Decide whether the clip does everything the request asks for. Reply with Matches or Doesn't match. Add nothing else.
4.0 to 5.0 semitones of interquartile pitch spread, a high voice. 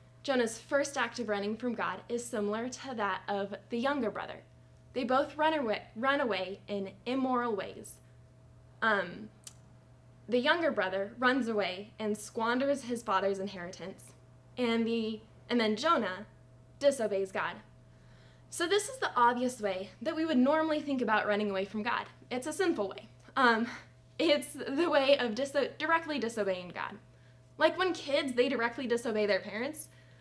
Doesn't match